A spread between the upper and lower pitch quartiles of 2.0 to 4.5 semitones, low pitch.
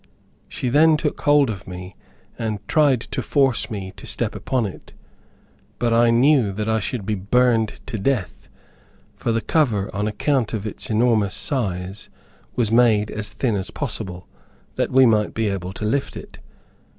Yes: average, 3.7 semitones; low, 110 Hz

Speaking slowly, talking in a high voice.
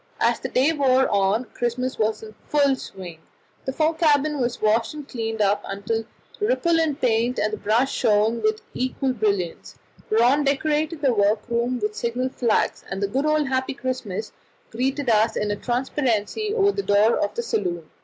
No: average, 175 wpm; high, 245 Hz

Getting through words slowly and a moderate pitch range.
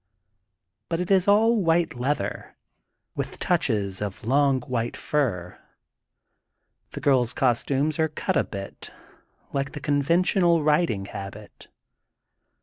No: slow, 125 wpm; wide, 6.8 semitones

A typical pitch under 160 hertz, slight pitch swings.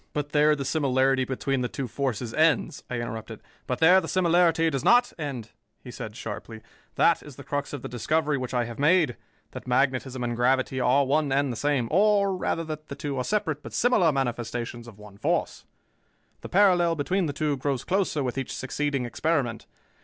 No: medium, 140 Hz; average, 4.3 semitones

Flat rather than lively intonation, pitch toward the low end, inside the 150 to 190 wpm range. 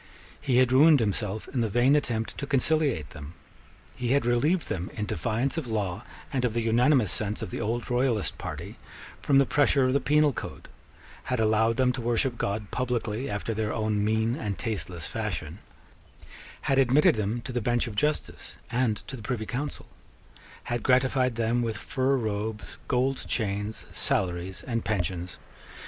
No: average, 3.5 semitones; low, 115 Hz; average, 170 wpm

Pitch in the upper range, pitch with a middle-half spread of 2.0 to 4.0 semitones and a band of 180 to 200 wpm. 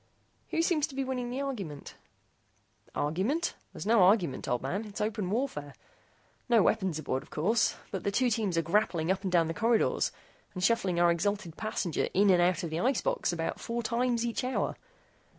No: high, 205 Hz; wide, 5.6 semitones; average, 190 wpm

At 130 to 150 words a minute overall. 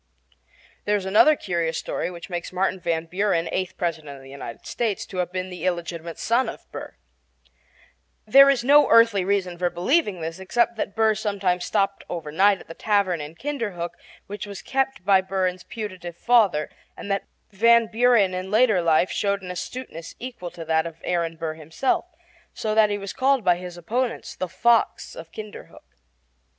No: average, 185 wpm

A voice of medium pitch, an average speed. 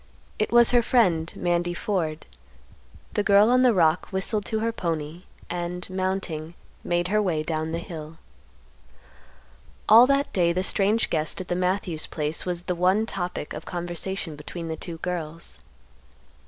Yes: medium, 175 Hz; average, 155 wpm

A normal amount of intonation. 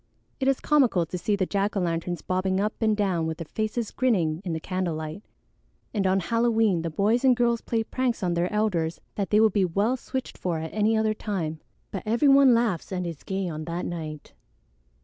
Yes: average, 4.6 semitones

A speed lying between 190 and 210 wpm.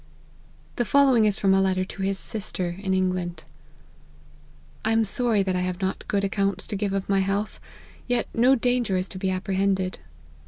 Yes: average, 195 wpm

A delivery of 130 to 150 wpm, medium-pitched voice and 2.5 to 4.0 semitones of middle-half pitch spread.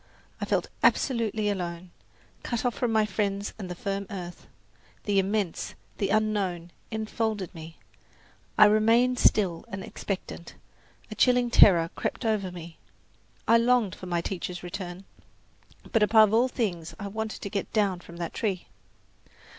No: average, 145 wpm; high, 200 Hz; average, 3.5 semitones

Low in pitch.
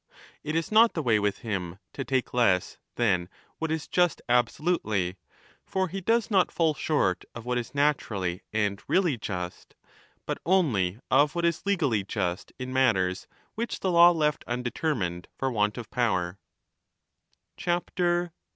Yes: low, 125 Hz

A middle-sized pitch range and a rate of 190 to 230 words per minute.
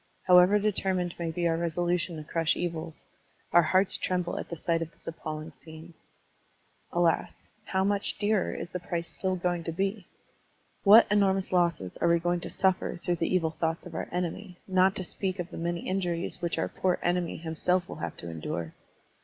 No: narrow, 2.0 semitones; average, 195 wpm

